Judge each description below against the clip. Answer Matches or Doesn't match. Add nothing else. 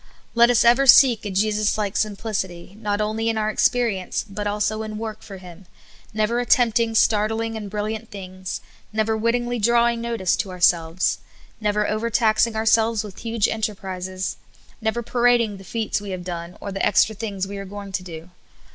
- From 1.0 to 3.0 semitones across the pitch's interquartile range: Matches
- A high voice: Matches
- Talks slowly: Doesn't match